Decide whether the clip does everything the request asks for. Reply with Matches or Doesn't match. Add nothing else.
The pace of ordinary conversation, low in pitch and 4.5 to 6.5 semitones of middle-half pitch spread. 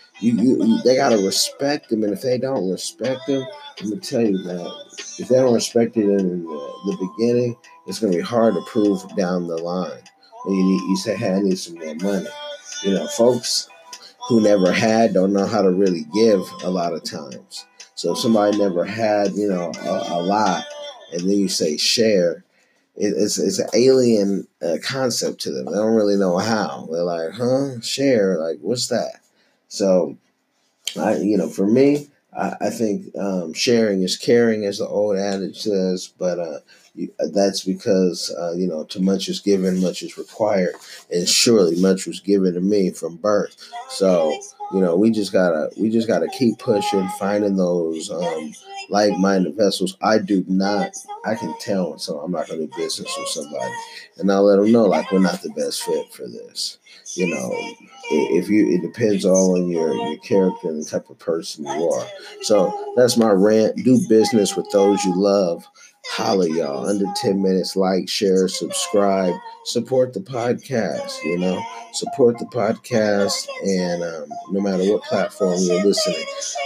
Matches